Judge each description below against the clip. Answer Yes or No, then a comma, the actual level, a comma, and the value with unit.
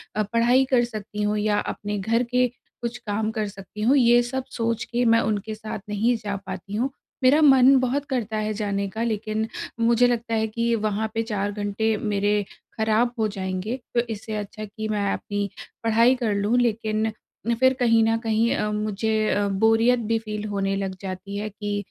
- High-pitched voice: Yes, high, 220 Hz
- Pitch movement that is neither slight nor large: No, narrow, 2.2 semitones